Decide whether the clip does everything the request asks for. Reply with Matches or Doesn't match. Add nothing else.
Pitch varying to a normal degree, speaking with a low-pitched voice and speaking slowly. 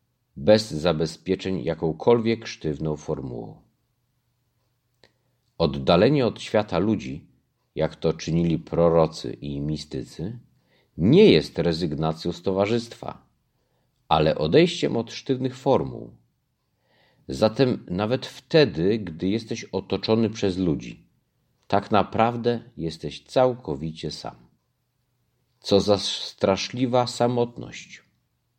Doesn't match